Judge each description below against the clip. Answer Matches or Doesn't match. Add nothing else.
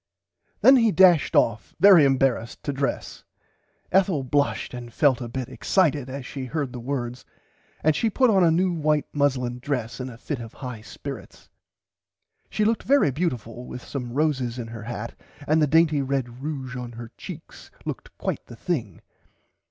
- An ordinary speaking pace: Matches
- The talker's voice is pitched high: Doesn't match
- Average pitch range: Matches